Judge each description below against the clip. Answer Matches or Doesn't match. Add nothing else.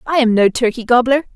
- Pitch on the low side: Doesn't match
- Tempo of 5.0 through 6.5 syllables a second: Matches